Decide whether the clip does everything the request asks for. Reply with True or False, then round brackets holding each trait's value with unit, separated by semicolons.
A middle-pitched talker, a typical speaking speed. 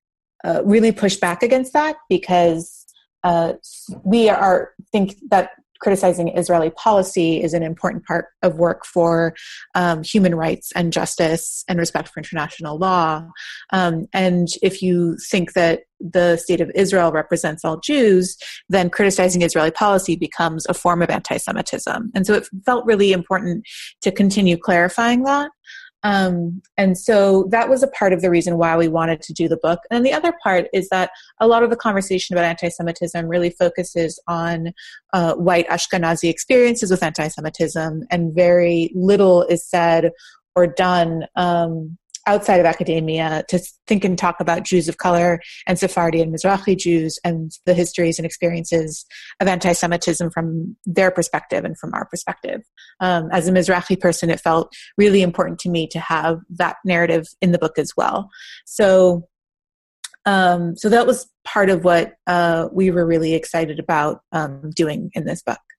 True (175 Hz; 165 wpm)